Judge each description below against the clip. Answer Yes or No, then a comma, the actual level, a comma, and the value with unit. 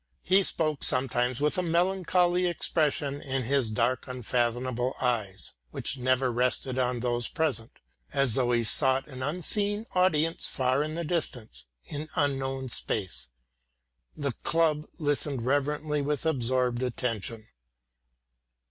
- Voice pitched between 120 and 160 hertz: Yes, low, 135 Hz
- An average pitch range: Yes, average, 3.8 semitones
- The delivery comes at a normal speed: No, slow, 125 wpm